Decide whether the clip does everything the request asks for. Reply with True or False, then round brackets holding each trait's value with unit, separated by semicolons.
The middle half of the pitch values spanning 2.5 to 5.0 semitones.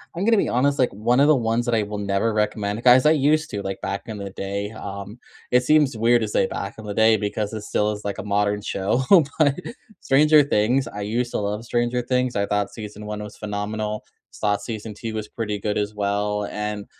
True (2.9 semitones)